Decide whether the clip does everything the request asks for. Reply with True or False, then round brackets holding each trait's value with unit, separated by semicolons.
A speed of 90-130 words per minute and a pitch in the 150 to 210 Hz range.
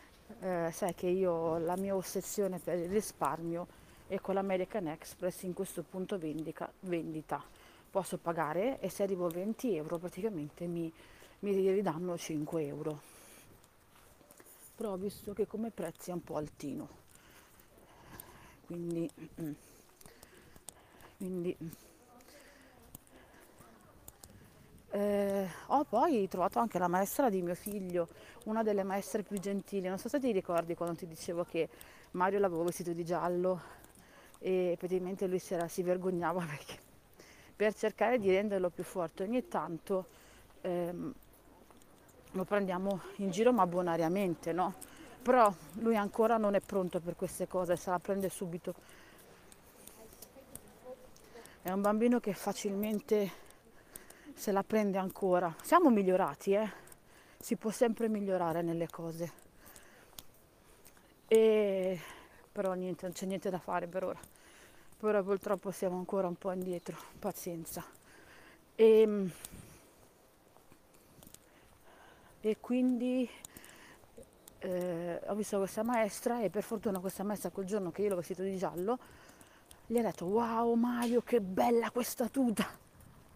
True (125 wpm; 190 Hz)